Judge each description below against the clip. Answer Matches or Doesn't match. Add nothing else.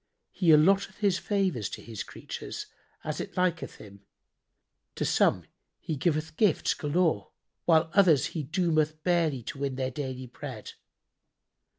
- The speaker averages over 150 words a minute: Doesn't match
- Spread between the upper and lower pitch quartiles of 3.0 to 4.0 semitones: Doesn't match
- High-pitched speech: Doesn't match